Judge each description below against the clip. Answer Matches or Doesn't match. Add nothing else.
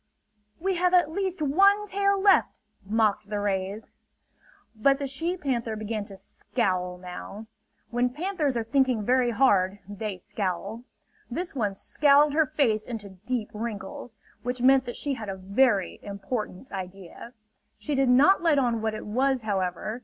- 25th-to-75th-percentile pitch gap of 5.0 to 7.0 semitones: Matches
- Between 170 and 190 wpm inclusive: Doesn't match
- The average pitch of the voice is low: Doesn't match